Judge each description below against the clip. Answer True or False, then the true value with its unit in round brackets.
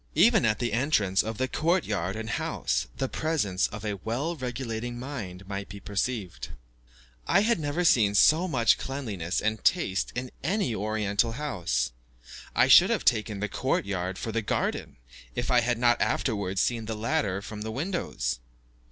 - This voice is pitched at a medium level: False (110 Hz)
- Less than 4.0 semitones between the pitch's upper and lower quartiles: False (4.7 semitones)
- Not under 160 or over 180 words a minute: True (170 wpm)